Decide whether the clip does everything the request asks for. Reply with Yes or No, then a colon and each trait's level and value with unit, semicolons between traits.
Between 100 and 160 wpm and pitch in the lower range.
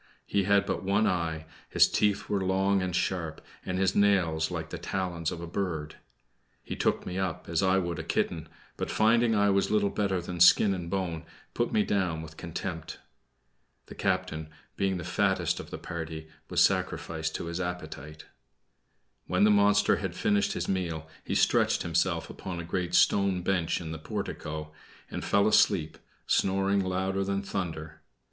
No: average, 175 wpm; very low, 90 Hz